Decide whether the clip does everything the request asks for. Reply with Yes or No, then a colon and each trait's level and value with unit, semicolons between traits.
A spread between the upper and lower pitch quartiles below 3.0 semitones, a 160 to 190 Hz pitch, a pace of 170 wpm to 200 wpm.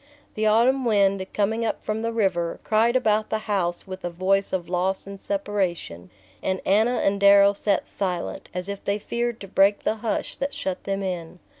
No: narrow, 2.4 semitones; high, 200 Hz; average, 190 wpm